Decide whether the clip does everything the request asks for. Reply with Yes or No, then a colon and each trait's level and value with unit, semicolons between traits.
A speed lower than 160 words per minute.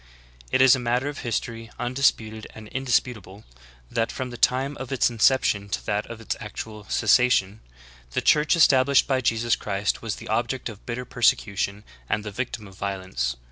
No: average, 175 wpm